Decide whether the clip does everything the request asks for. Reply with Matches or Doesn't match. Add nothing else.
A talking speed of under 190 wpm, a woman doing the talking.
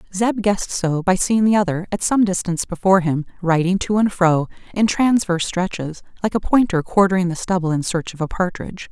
Doesn't match